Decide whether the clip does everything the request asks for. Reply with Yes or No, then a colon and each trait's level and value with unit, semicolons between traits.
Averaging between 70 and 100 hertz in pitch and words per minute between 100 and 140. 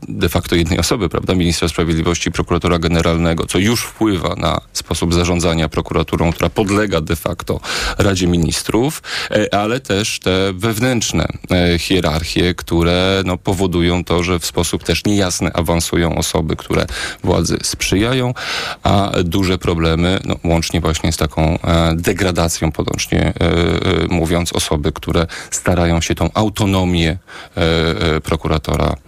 Yes: very low, 85 Hz; average, 120 wpm